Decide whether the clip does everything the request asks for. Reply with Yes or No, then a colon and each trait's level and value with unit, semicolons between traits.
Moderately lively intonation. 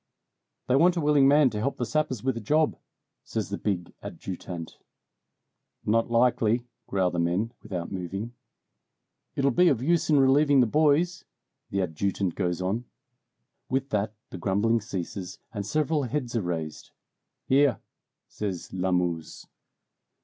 No: wide, 6.7 semitones